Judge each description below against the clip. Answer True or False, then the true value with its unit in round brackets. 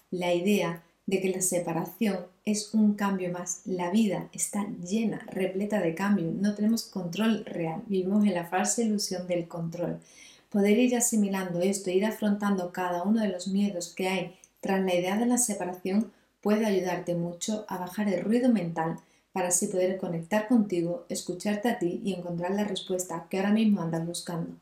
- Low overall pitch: False (190 Hz)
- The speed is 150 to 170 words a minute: False (180 wpm)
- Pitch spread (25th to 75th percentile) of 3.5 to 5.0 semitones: False (2.9 semitones)